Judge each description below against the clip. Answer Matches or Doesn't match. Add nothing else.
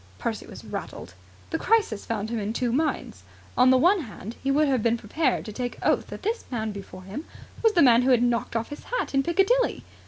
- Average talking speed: Doesn't match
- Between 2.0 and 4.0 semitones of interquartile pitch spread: Doesn't match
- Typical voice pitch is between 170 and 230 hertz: Doesn't match